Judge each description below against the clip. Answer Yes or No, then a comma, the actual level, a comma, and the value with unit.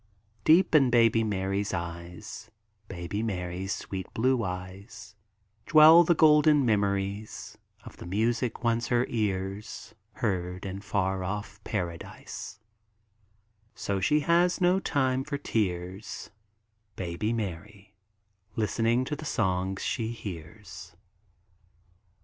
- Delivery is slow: Yes, slow, 110 wpm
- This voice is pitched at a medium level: No, low, 105 Hz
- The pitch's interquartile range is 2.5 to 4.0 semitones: No, average, 4.4 semitones